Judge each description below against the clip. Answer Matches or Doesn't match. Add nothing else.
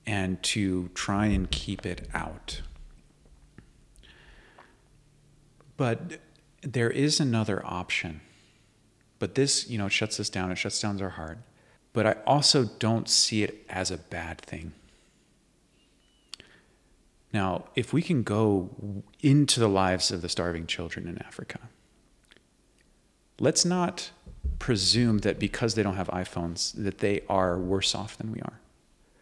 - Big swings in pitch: Doesn't match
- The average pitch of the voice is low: Matches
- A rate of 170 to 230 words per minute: Doesn't match